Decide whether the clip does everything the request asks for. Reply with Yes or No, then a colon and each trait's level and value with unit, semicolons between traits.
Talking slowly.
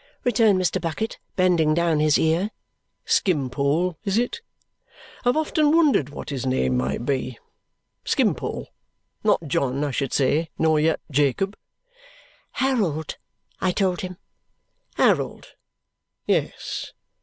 Yes: slow, 115 wpm